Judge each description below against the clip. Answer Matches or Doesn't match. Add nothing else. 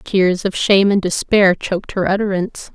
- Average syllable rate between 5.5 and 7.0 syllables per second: Doesn't match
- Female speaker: Matches